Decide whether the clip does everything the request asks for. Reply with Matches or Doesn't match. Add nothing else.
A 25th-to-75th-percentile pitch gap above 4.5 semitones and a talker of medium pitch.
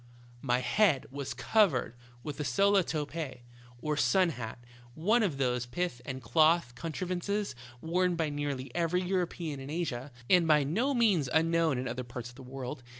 Matches